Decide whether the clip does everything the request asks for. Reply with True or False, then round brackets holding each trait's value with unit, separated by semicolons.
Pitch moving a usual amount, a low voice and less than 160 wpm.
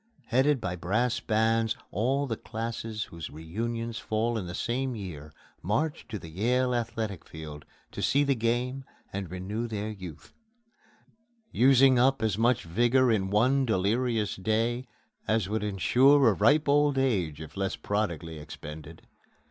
True (4.6 semitones; 110 Hz; 150 wpm)